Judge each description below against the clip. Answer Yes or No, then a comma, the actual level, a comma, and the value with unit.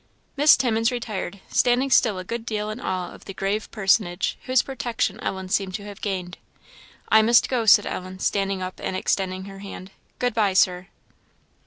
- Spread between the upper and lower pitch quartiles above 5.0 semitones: No, average, 3.4 semitones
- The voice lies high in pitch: Yes, high, 200 Hz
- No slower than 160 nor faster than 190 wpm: Yes, average, 180 wpm